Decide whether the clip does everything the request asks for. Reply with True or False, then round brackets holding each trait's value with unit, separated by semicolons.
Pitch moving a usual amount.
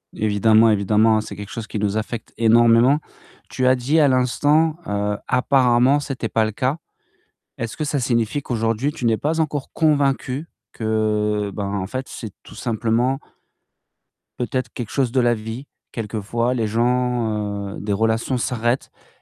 True (3.0 semitones)